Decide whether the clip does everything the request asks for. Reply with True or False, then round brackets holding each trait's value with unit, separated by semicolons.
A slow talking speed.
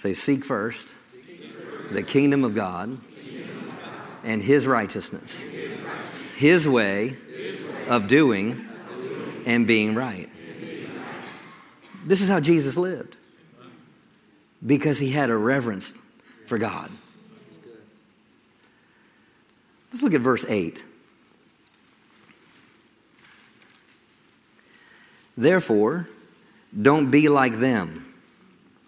True (80 wpm)